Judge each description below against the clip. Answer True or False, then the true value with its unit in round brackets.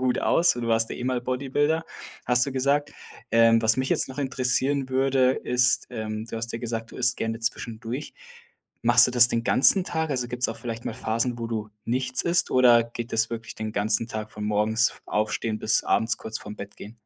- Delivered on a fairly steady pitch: True (2.3 semitones)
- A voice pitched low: True (120 Hz)